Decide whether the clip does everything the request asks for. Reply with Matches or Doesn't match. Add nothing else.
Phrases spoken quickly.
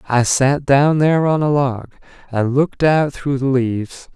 Doesn't match